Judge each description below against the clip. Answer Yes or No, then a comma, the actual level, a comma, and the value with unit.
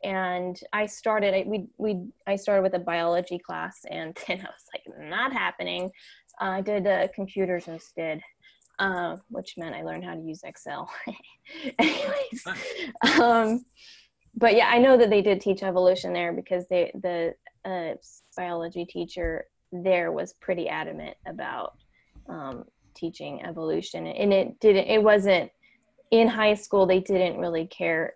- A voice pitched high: Yes, high, 195 Hz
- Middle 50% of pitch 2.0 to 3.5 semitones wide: No, average, 4.2 semitones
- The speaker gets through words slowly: No, average, 155 wpm